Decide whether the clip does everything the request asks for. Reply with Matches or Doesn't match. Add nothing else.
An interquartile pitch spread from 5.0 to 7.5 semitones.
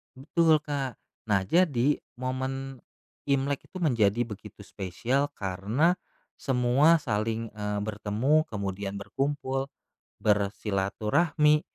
Matches